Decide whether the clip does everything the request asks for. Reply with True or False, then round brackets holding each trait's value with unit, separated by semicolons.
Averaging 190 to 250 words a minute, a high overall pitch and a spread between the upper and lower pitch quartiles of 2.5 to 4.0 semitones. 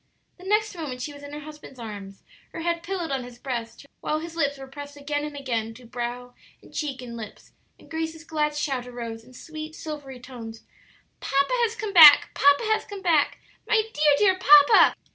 False (200 wpm; 285 Hz; 4.4 semitones)